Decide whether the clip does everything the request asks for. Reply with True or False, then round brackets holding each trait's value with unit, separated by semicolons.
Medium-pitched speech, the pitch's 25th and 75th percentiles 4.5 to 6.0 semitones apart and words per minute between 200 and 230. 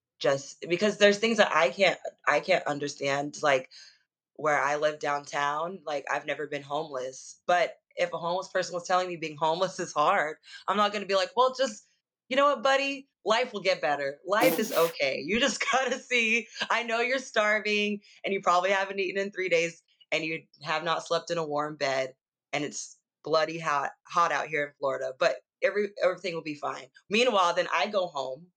True (175 Hz; 5.6 semitones; 205 wpm)